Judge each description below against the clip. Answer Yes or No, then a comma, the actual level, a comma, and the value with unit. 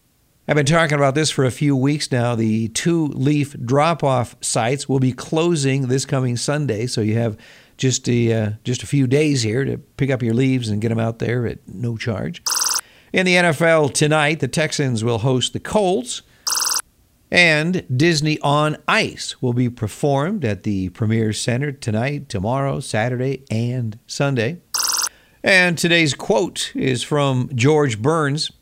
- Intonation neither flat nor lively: Yes, average, 4.1 semitones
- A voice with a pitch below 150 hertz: Yes, low, 135 Hz